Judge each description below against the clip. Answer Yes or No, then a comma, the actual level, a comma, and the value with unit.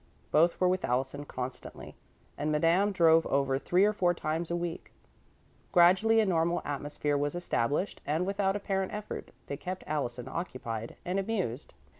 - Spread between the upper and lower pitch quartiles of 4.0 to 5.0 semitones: Yes, average, 4.5 semitones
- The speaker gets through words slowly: No, average, 155 wpm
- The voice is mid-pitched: Yes, medium, 170 Hz